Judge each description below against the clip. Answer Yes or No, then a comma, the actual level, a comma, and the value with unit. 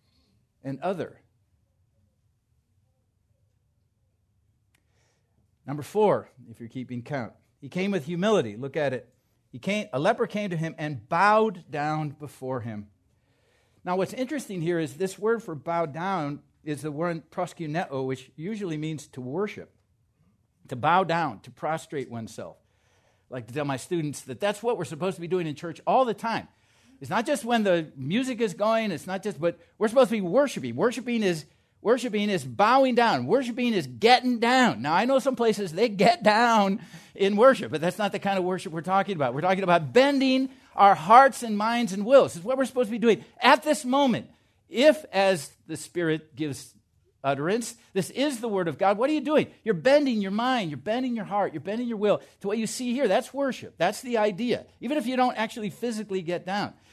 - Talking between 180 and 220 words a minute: Yes, average, 195 wpm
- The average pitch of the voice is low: No, medium, 185 Hz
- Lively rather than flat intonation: Yes, wide, 8.5 semitones